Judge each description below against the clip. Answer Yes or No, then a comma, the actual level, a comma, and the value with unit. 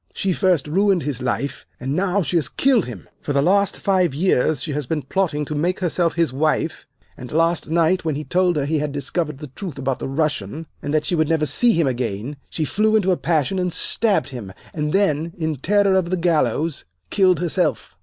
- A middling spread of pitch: Yes, average, 4.1 semitones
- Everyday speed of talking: No, fast, 215 wpm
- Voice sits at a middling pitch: Yes, medium, 160 Hz